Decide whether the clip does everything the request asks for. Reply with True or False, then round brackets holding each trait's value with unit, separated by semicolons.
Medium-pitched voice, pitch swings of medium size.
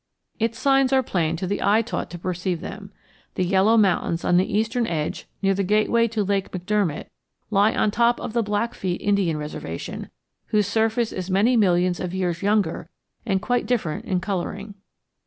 False (200 Hz; 3.5 semitones)